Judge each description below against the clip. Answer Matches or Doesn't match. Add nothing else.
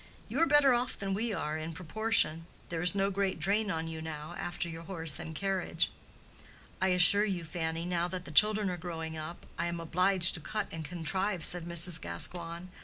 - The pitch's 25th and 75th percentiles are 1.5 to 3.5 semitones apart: Matches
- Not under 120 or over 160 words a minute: Doesn't match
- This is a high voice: Doesn't match